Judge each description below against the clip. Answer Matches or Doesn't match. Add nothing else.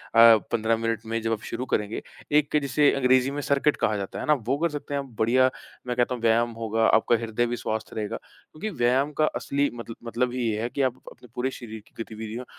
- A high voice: Doesn't match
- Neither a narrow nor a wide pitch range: Matches